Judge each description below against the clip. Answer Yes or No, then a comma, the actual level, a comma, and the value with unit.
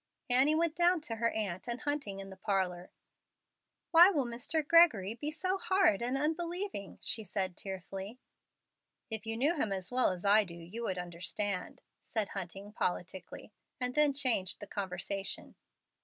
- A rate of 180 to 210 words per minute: No, average, 160 wpm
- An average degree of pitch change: No, wide, 7.4 semitones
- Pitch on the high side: Yes, high, 220 Hz